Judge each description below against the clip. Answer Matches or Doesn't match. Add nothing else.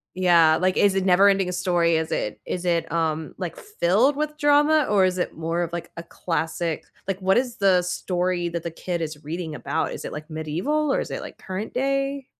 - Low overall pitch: Doesn't match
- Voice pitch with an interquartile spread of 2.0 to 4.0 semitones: Matches